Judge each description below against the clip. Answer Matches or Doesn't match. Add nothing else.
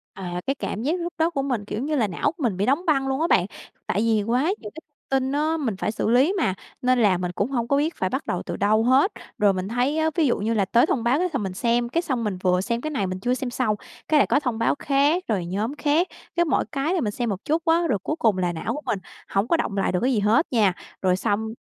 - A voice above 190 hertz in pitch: Matches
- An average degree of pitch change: Doesn't match